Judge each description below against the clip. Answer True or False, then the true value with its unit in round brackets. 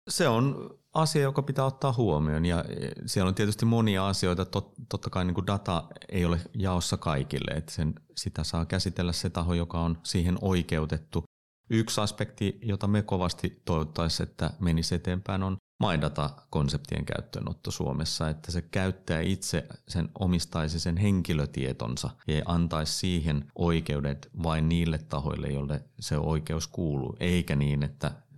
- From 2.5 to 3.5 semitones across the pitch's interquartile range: False (3.9 semitones)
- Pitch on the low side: True (90 Hz)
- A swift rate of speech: False (135 wpm)